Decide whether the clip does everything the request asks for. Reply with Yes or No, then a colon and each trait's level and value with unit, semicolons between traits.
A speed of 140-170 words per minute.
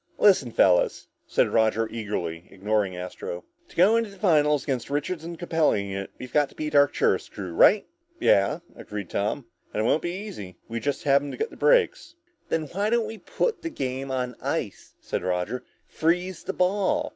No: average, 190 wpm